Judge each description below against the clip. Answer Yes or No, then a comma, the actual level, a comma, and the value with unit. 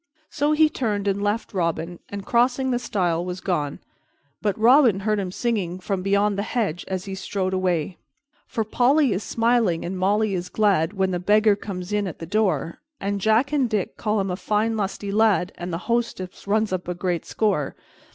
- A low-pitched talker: No, high, 200 Hz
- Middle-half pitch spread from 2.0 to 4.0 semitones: Yes, average, 3.2 semitones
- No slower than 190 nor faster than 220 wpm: Yes, average, 195 wpm